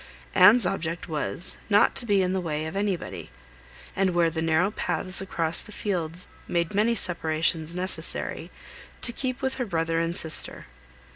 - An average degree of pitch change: Yes, average, 3.6 semitones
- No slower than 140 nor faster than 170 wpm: Yes, average, 160 wpm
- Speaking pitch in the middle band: Yes, medium, 180 Hz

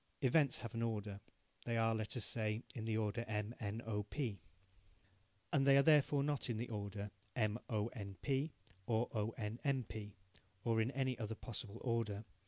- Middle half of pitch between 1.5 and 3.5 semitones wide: Yes, average, 3.0 semitones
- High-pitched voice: No, low, 115 Hz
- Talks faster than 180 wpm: Yes, average, 190 wpm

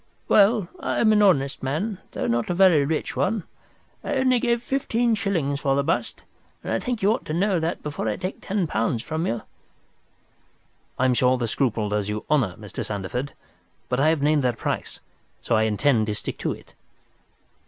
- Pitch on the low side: No, medium, 150 Hz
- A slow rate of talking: No, average, 195 wpm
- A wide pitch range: Yes, wide, 8.6 semitones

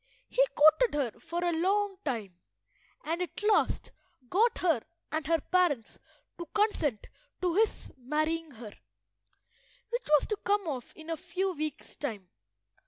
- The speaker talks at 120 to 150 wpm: Yes, average, 145 wpm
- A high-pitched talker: Yes, very high, 330 Hz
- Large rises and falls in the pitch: No, average, 4.7 semitones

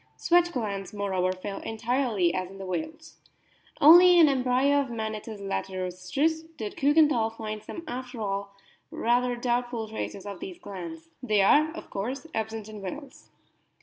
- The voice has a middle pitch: No, high, 225 Hz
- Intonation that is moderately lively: No, wide, 5.7 semitones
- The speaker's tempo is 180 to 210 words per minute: No, average, 150 wpm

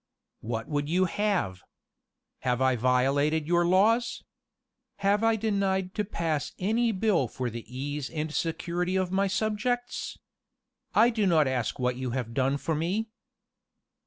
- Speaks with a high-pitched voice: No, medium, 170 Hz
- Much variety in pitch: Yes, wide, 7.4 semitones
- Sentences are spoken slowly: No, average, 150 wpm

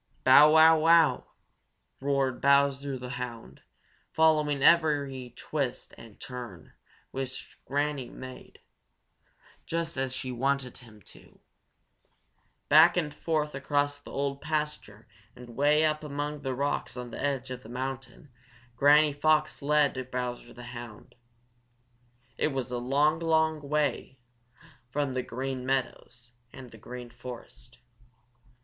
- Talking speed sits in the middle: No, slow, 130 wpm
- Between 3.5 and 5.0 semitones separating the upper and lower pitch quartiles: No, average, 3.1 semitones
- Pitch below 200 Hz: Yes, low, 135 Hz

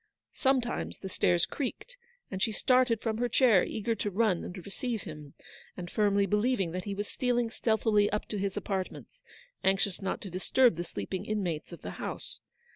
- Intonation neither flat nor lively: Yes, average, 3.7 semitones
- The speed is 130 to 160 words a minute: No, average, 190 wpm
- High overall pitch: Yes, high, 205 Hz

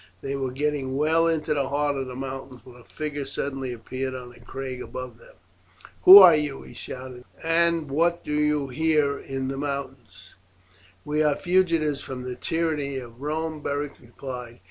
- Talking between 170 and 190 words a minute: Yes, average, 175 wpm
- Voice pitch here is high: No, medium, 140 Hz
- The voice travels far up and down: No, average, 2.8 semitones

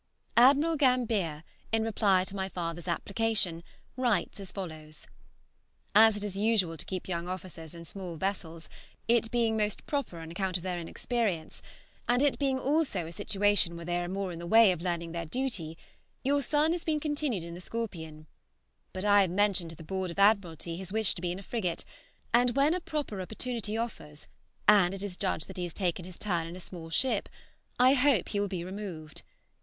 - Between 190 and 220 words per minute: Yes, average, 200 wpm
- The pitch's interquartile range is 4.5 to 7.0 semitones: Yes, average, 5.0 semitones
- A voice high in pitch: Yes, high, 195 Hz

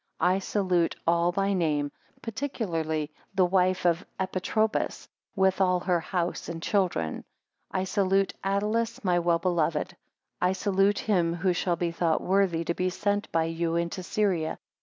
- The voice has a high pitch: No, medium, 180 Hz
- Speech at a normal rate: Yes, average, 160 wpm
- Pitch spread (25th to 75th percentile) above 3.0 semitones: No, narrow, 2.5 semitones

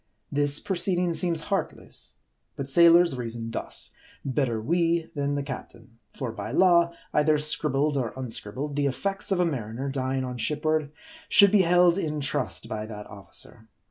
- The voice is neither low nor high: Yes, medium, 145 Hz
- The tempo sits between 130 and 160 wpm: Yes, average, 155 wpm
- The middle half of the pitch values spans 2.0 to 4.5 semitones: No, average, 5.2 semitones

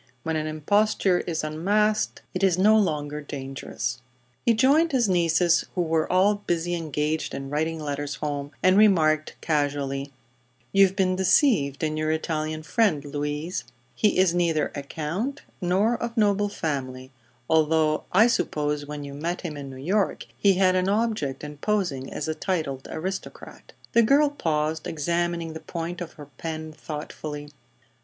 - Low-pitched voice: No, medium, 160 Hz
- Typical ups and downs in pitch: Yes, average, 4.4 semitones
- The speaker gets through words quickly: No, average, 155 wpm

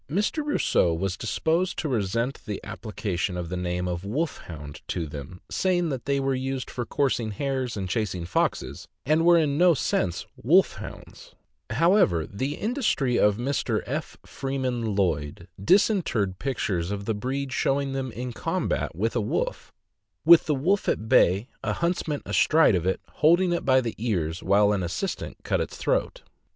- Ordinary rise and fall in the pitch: No, wide, 7.6 semitones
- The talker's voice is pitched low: Yes, low, 120 Hz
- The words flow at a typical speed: Yes, average, 165 wpm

